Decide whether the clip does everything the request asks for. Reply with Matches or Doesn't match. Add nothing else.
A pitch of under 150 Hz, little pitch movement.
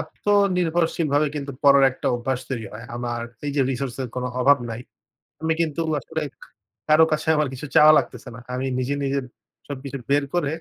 Doesn't match